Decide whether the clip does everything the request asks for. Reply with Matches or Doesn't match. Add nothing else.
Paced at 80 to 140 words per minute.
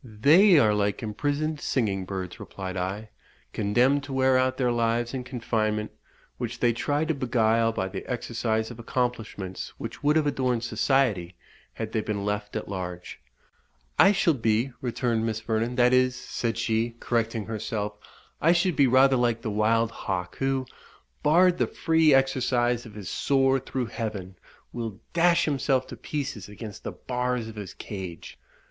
Doesn't match